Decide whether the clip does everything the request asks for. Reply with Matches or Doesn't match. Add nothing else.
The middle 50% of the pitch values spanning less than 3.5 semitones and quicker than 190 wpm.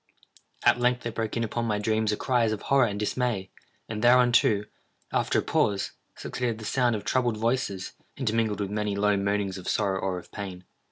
Matches